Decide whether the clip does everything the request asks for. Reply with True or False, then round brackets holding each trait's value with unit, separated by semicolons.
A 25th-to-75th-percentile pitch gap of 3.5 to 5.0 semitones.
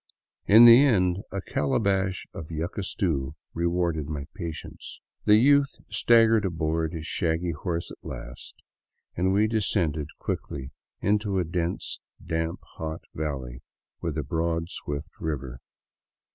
True (4.0 semitones)